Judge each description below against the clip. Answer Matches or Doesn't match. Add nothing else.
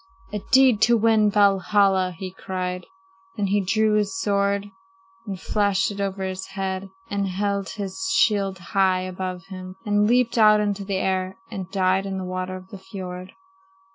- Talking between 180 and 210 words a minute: Doesn't match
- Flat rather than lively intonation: Matches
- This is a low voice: Doesn't match